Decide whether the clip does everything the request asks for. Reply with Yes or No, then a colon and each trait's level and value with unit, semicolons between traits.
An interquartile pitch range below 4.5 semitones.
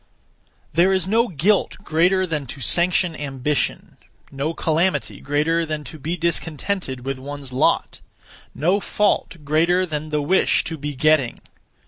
Yes: average, 3.6 semitones